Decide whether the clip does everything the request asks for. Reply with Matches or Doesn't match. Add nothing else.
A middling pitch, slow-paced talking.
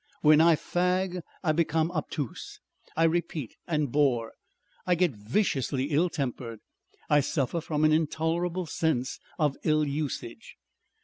Matches